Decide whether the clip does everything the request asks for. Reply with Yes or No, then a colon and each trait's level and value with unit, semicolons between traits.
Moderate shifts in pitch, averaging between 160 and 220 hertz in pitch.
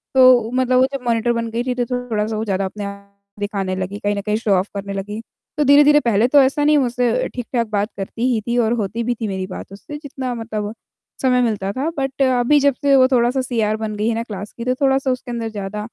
No: average, 3.7 semitones; high, 230 Hz